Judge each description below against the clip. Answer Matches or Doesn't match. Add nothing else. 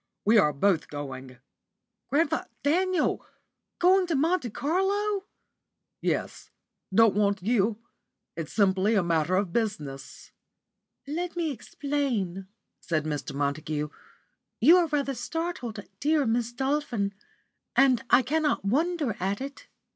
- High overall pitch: Matches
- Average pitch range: Doesn't match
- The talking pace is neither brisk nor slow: Doesn't match